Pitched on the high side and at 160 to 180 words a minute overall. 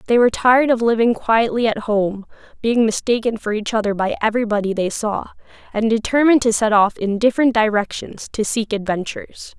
Yes: high, 225 Hz; average, 175 wpm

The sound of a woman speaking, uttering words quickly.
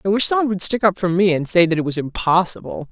Yes: female; fast, 290 wpm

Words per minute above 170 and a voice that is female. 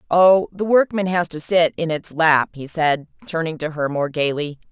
Yes: fast, 205 wpm; female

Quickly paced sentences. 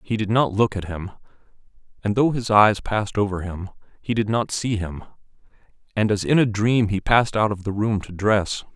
Yes: fast, 215 wpm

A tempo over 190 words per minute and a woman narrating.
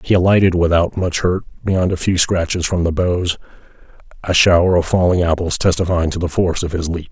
No: average, 200 wpm; male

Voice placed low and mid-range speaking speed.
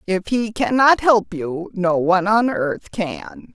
No: high, 200 Hz; average, 170 wpm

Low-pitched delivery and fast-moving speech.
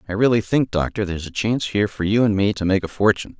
Yes: low, 100 Hz; fast, 285 wpm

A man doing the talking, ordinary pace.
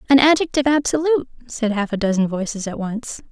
No: female; average, 180 wpm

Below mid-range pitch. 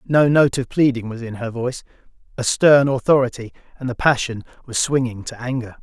Yes: low, 125 Hz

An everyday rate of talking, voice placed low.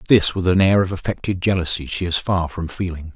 No: fast, 230 wpm; very low, 90 Hz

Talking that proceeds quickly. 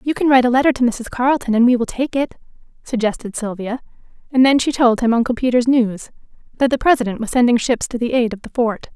Yes: fast, 235 wpm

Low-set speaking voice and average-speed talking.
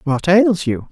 No: medium, 170 Hz; average, 195 wpm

